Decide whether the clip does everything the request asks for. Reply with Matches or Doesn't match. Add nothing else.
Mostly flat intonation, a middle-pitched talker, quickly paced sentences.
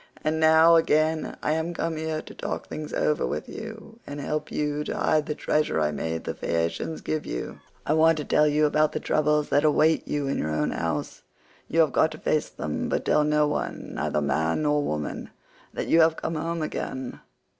Matches